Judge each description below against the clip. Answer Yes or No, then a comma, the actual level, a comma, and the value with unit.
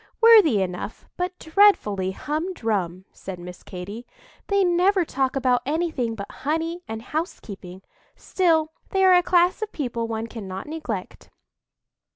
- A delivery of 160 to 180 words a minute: No, slow, 135 wpm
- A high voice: Yes, very high, 270 Hz